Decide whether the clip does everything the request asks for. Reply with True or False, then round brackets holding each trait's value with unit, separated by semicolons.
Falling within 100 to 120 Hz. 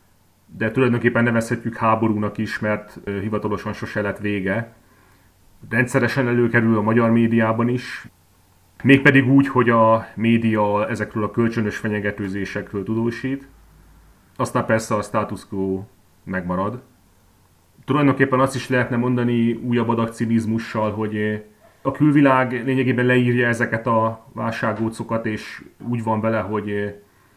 True (110 Hz)